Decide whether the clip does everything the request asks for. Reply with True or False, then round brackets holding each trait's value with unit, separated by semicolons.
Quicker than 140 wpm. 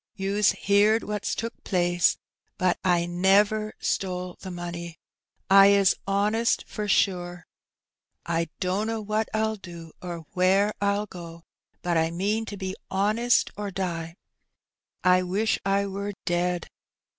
False (135 wpm)